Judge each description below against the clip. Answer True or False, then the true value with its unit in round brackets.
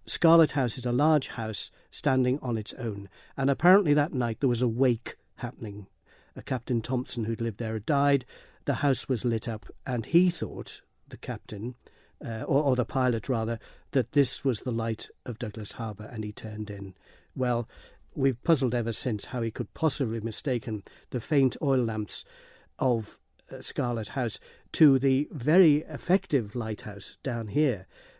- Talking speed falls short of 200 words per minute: True (170 wpm)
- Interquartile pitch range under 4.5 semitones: True (3.3 semitones)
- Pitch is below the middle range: True (125 Hz)